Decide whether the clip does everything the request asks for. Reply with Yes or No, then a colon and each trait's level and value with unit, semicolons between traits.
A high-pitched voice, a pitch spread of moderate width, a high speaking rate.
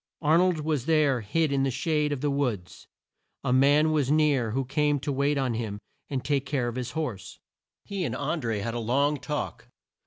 No: medium, 140 Hz; average, 3.2 semitones; fast, 210 wpm